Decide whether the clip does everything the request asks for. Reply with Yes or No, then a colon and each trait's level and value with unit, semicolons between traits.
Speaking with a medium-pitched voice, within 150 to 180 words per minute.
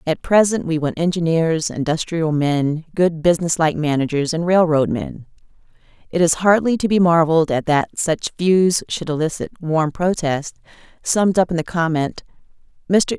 Yes: medium, 165 Hz; average, 155 wpm